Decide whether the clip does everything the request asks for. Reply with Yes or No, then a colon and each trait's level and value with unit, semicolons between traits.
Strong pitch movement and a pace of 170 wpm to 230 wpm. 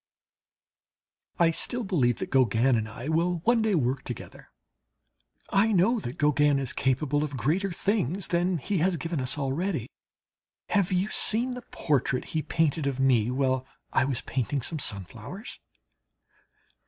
No: wide, 6.0 semitones; average, 150 wpm